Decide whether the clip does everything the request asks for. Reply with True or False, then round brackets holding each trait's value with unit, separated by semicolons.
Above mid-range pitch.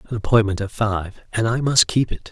False (110 Hz)